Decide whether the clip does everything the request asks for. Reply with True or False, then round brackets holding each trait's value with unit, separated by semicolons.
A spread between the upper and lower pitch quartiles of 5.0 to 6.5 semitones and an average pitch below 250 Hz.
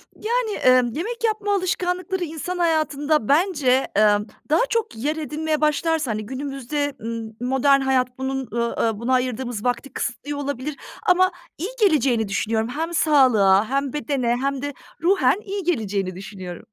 False (5.4 semitones; 275 Hz)